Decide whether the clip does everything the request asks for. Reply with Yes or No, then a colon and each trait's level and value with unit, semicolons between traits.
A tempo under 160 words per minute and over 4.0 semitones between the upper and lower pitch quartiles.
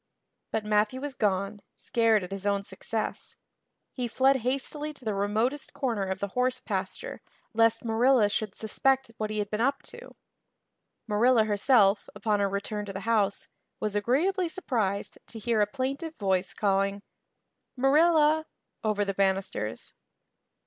Yes: average, 150 wpm; average, 4.4 semitones